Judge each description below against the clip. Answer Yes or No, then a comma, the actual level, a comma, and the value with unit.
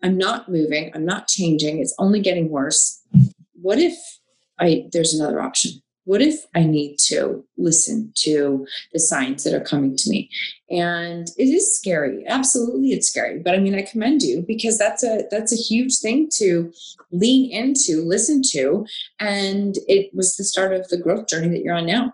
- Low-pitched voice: No, high, 195 Hz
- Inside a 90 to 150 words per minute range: No, average, 185 wpm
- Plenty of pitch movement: Yes, wide, 6.0 semitones